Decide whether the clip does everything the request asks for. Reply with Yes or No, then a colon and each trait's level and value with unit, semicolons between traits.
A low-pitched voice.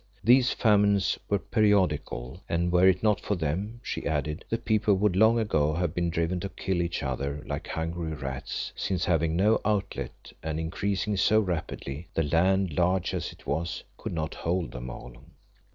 Yes: very low, 90 Hz